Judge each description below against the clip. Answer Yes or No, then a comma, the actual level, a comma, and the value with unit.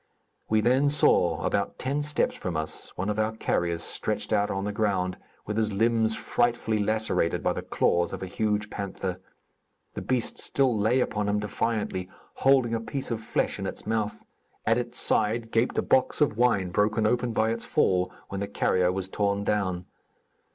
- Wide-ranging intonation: No, average, 3.0 semitones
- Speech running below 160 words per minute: No, average, 185 wpm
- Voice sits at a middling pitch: No, low, 110 Hz